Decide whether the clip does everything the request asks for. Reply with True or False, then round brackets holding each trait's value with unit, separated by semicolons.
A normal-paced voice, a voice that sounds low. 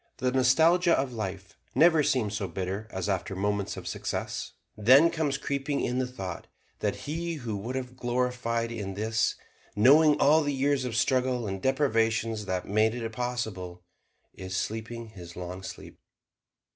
True (160 wpm; 115 Hz)